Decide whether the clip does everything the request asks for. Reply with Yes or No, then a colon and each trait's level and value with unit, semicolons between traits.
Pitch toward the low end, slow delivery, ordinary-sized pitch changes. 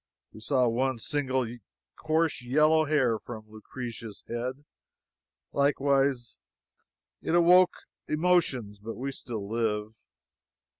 Yes: low, 130 Hz; slow, 100 wpm; average, 4.4 semitones